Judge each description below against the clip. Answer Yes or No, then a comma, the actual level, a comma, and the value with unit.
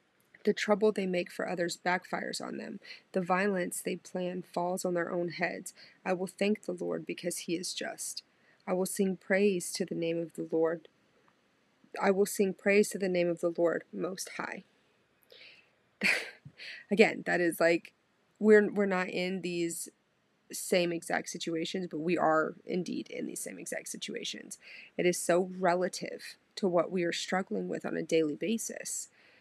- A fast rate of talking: No, average, 170 wpm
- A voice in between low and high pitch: Yes, medium, 180 Hz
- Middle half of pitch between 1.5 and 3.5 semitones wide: Yes, average, 2.8 semitones